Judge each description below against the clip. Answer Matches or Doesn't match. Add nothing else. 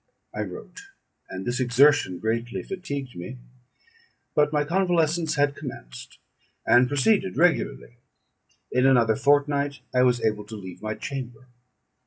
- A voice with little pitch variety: Doesn't match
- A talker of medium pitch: Doesn't match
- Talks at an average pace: Doesn't match